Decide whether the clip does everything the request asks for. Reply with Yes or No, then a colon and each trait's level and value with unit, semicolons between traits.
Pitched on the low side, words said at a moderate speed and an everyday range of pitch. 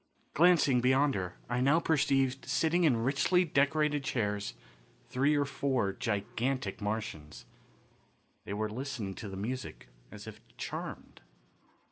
No: low, 130 Hz; slow, 125 wpm; average, 5.0 semitones